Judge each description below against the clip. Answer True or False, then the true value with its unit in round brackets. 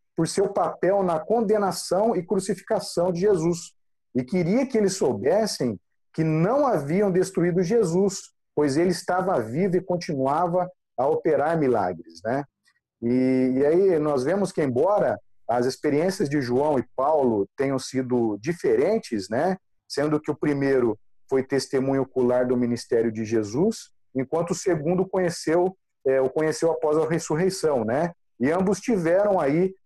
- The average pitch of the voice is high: False (165 Hz)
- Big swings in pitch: True (6.1 semitones)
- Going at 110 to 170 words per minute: True (145 wpm)